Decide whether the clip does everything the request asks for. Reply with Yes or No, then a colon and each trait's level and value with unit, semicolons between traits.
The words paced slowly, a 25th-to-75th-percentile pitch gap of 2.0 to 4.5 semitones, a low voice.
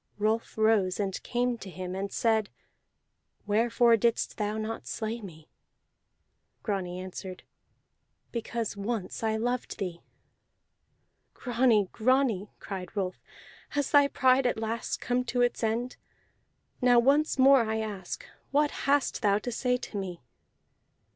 No: slow, 130 wpm; average, 3.6 semitones; high, 225 Hz